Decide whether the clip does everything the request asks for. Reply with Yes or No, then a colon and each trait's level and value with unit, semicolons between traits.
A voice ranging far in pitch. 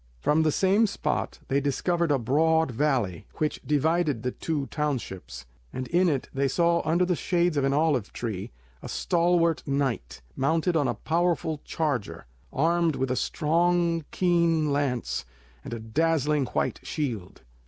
No: average, 3.8 semitones